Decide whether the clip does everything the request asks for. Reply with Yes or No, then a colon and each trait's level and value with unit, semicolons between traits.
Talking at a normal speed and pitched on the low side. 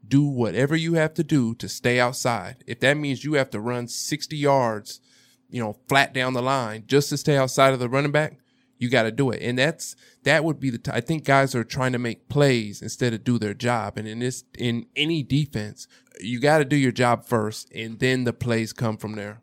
No: fast, 240 wpm; low, 125 Hz